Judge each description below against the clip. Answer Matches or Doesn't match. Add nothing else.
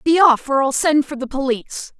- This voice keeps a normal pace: Doesn't match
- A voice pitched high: Matches